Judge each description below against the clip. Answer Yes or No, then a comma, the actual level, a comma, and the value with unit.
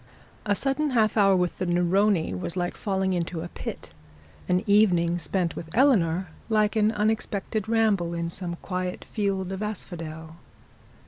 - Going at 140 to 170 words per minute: Yes, average, 150 wpm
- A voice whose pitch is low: No, high, 190 Hz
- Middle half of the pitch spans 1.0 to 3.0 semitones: No, average, 3.5 semitones